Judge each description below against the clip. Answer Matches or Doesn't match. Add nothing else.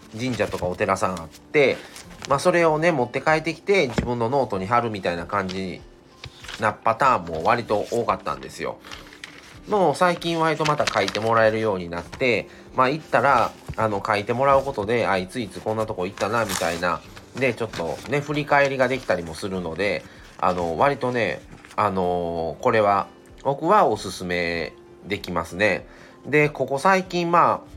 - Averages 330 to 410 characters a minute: Matches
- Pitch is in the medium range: Doesn't match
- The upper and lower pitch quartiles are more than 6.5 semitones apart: Matches